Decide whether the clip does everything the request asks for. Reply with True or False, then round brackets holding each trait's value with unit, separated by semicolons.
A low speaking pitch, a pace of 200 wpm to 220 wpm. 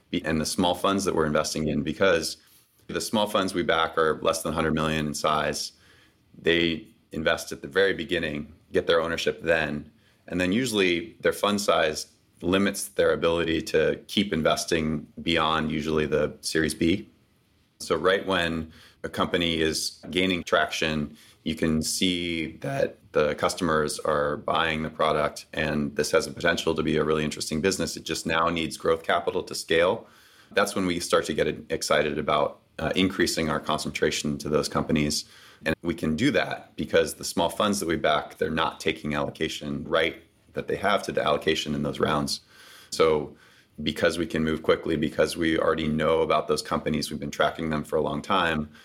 False (80 Hz; 180 wpm)